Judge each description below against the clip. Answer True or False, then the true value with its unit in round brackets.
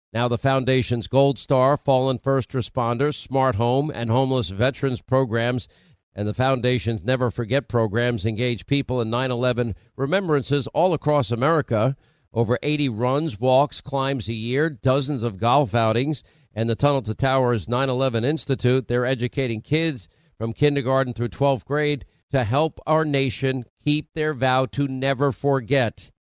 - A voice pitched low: True (130 Hz)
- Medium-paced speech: True (150 wpm)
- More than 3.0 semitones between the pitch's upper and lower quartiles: False (2.7 semitones)